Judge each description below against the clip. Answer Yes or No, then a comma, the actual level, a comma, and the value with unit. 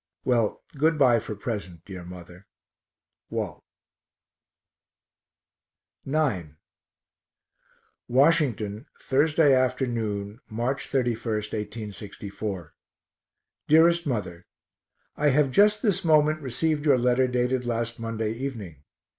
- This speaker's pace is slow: Yes, slow, 90 wpm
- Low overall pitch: Yes, low, 120 Hz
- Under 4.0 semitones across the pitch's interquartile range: No, average, 5.3 semitones